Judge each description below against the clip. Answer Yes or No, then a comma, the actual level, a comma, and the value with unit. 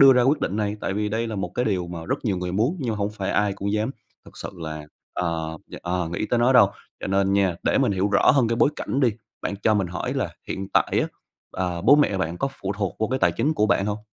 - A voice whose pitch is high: No, low, 100 Hz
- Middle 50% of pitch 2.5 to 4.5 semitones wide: Yes, average, 4.0 semitones